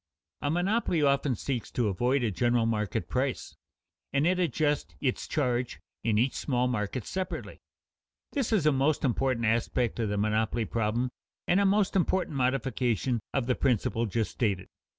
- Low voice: Yes, low, 125 Hz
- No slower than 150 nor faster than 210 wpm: Yes, average, 160 wpm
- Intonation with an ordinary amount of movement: Yes, average, 4.3 semitones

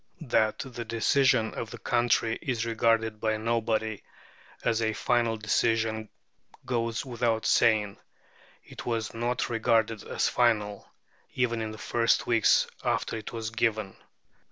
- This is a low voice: Yes, low, 115 Hz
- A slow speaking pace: Yes, slow, 130 wpm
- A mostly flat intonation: Yes, narrow, 1.2 semitones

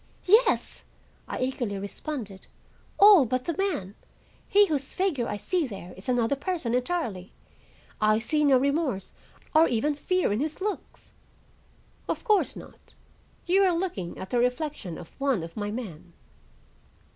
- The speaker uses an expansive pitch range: Yes, wide, 8.4 semitones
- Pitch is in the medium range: No, very high, 260 Hz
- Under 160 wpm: Yes, average, 145 wpm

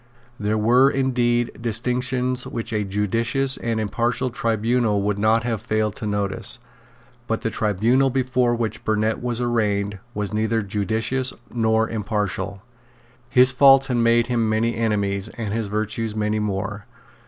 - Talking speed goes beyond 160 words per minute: No, average, 140 wpm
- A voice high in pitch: No, low, 115 Hz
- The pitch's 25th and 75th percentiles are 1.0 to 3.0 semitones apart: Yes, narrow, 2.4 semitones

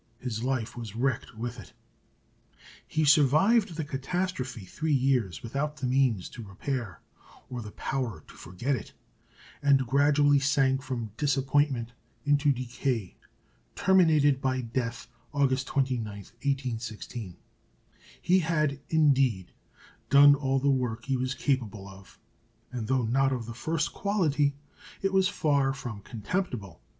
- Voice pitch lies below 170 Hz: Yes, low, 135 Hz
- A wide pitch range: No, average, 3.6 semitones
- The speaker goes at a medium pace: No, slow, 130 wpm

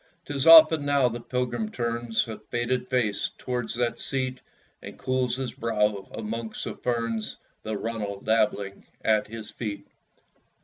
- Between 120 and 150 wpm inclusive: Yes, average, 140 wpm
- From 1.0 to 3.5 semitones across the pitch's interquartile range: Yes, narrow, 2.5 semitones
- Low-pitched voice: Yes, low, 115 Hz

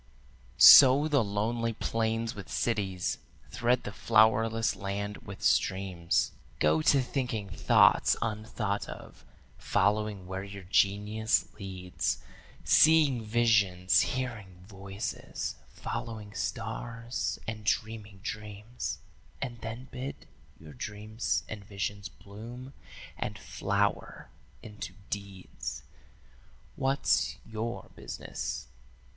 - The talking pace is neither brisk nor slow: No, slow, 95 wpm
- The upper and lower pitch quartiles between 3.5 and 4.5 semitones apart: No, average, 2.7 semitones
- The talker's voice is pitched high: No, low, 110 Hz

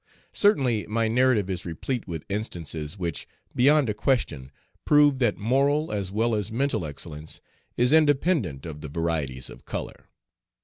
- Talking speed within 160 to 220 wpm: No, average, 145 wpm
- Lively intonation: Yes, wide, 8.1 semitones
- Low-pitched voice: Yes, low, 105 Hz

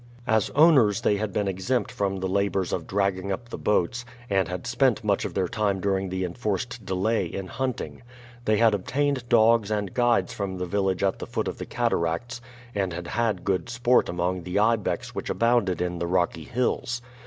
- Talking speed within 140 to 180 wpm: No, average, 195 wpm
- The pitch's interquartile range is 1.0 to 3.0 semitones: No, average, 4.0 semitones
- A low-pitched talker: Yes, low, 100 Hz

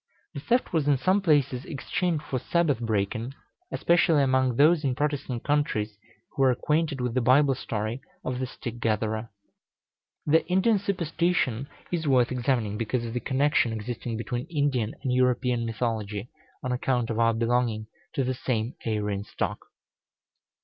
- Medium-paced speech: Yes, average, 155 wpm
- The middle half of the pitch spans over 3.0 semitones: Yes, average, 4.1 semitones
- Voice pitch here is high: No, low, 125 Hz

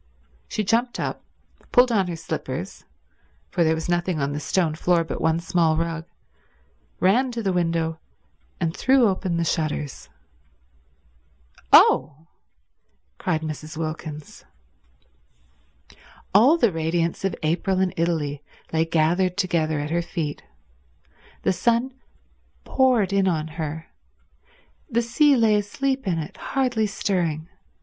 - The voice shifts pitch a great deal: No, average, 4.2 semitones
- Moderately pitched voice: Yes, medium, 170 Hz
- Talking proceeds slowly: Yes, slow, 125 wpm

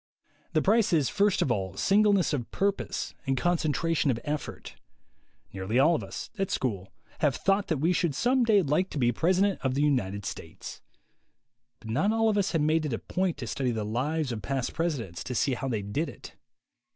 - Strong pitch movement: Yes, wide, 7.2 semitones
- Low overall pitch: No, medium, 150 Hz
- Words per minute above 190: Yes, average, 200 wpm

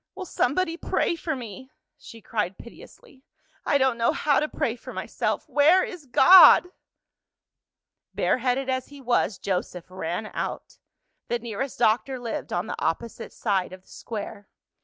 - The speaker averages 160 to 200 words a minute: No, average, 150 wpm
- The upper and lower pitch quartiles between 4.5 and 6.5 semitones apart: Yes, average, 4.9 semitones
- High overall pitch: Yes, high, 245 Hz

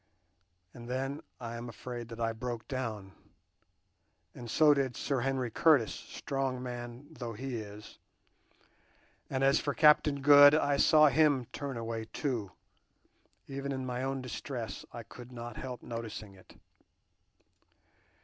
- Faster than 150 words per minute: No, average, 140 wpm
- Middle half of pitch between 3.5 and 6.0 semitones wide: No, average, 2.9 semitones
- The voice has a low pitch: Yes, low, 125 Hz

